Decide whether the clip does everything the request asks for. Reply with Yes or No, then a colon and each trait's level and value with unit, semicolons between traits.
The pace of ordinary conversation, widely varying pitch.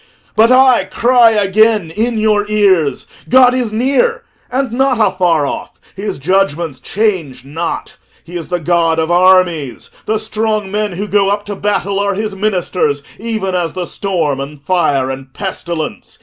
No: average, 160 wpm; average, 4.4 semitones